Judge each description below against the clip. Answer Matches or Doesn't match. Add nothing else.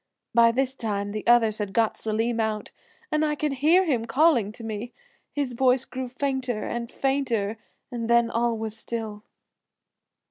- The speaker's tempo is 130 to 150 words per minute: Doesn't match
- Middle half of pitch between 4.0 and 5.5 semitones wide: Doesn't match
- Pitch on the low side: Doesn't match